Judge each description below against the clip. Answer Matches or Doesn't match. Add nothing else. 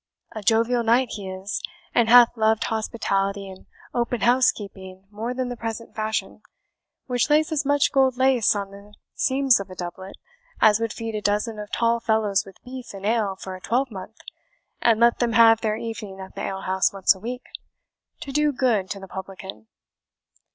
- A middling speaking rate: Matches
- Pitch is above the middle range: Matches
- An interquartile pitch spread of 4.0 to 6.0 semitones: Doesn't match